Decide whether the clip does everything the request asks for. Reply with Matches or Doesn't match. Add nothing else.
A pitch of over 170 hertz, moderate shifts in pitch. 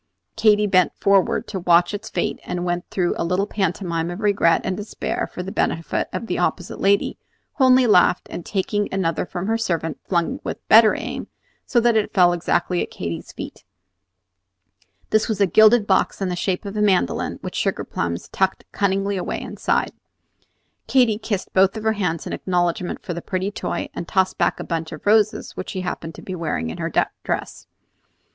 Matches